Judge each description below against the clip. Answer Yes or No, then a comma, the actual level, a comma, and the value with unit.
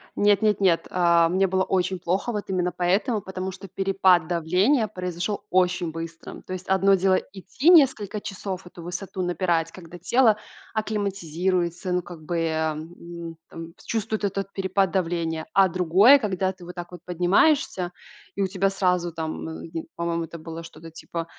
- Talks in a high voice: No, medium, 180 Hz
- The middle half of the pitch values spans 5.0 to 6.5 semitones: No, narrow, 2.4 semitones